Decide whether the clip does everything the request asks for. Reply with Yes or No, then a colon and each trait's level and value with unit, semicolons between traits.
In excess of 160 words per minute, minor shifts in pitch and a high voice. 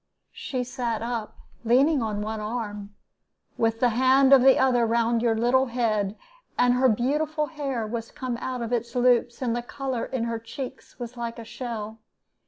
Yes: average, 180 wpm; narrow, 2.2 semitones; high, 240 Hz